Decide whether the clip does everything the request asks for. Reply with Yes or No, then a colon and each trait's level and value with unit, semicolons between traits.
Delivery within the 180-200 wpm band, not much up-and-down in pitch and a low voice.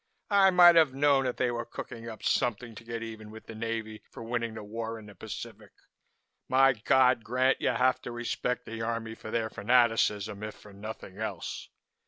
Yes: average, 195 wpm; narrow, 2.3 semitones; low, 115 Hz